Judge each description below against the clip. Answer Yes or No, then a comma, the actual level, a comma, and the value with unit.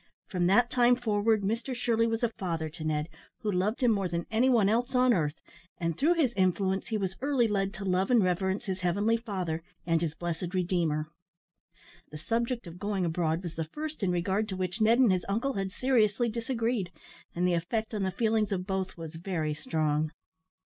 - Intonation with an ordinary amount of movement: Yes, average, 4.7 semitones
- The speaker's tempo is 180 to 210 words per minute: Yes, average, 200 wpm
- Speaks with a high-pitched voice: Yes, high, 195 Hz